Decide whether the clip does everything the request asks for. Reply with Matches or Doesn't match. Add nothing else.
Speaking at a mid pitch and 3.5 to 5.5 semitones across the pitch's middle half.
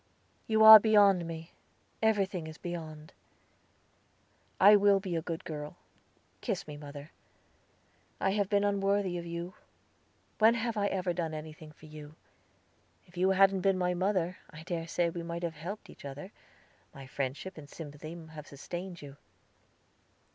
Matches